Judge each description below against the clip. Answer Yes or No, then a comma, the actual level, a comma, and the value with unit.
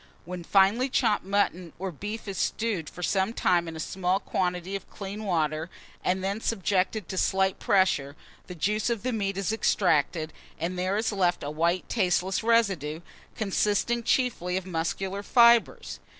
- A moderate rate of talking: Yes, average, 165 wpm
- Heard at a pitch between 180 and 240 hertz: Yes, high, 190 Hz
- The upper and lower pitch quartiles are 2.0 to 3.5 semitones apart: Yes, average, 3.0 semitones